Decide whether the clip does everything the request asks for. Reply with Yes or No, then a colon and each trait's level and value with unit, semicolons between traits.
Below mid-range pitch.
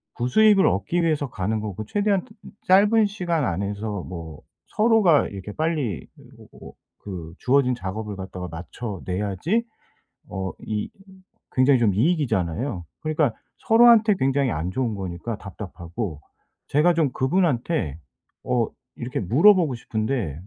Yes: low, 120 Hz